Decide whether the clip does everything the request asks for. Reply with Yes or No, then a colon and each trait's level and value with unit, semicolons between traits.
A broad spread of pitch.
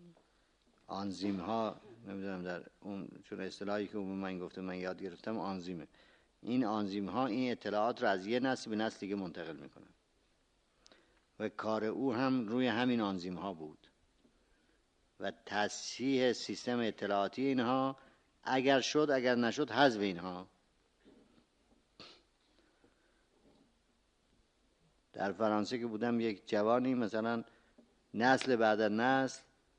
No: average, 4.2 semitones